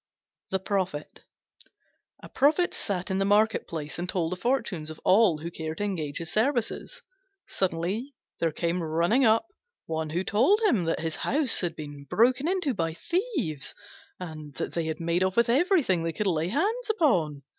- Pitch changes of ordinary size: No, wide, 6.8 semitones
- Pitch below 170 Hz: No, medium, 185 Hz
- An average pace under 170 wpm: No, average, 175 wpm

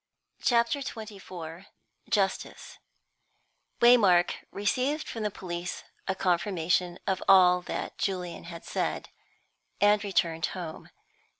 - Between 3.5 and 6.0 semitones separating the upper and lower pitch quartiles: No, average, 3.1 semitones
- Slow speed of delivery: Yes, slow, 100 wpm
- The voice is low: No, high, 190 Hz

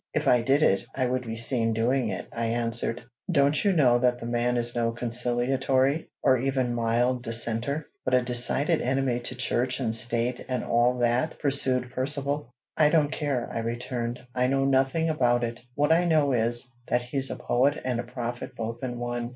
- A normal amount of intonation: No, narrow, 2.2 semitones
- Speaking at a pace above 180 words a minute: Yes, average, 190 wpm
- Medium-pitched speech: No, low, 125 Hz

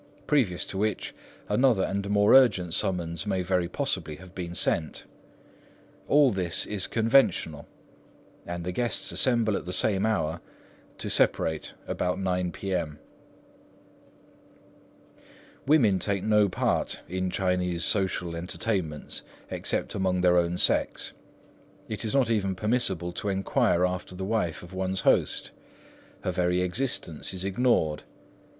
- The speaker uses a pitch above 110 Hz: No, very low, 95 Hz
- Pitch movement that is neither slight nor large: Yes, average, 3.1 semitones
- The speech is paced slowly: Yes, slow, 130 wpm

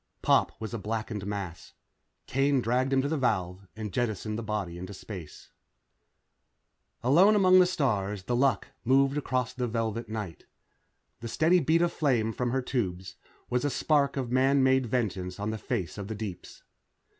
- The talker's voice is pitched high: No, low, 115 Hz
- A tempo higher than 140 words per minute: Yes, average, 175 wpm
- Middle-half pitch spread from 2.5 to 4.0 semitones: No, average, 4.7 semitones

